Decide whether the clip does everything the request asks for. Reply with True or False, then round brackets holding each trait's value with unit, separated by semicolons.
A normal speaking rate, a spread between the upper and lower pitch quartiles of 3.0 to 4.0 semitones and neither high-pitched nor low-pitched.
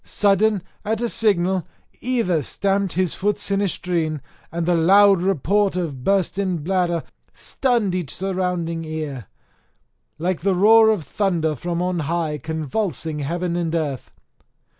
False (130 wpm; 3.4 semitones; 180 Hz)